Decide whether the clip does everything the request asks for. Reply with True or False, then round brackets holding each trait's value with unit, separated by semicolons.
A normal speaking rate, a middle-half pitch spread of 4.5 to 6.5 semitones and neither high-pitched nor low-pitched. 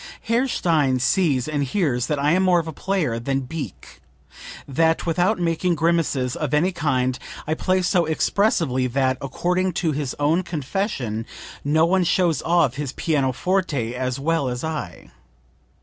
True (155 wpm; 5.0 semitones; 155 Hz)